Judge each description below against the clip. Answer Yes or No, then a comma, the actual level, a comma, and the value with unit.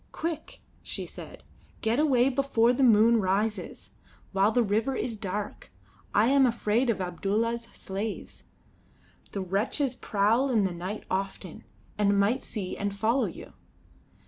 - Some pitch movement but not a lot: Yes, average, 3.5 semitones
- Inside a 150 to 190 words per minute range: No, average, 140 wpm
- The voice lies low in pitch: No, high, 220 Hz